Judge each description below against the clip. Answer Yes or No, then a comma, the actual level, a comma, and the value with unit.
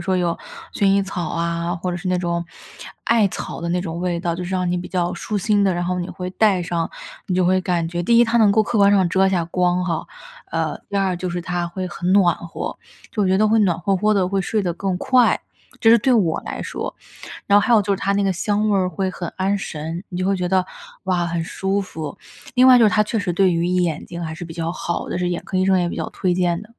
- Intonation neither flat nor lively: No, narrow, 2.3 semitones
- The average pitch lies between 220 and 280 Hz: No, medium, 185 Hz